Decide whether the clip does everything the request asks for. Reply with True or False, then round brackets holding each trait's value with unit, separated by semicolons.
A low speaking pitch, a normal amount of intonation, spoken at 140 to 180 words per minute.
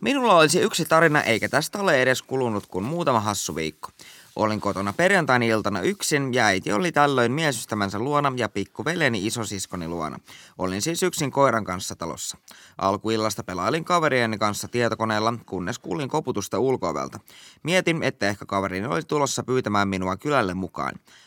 False (115 Hz; 6.3 semitones; 150 wpm)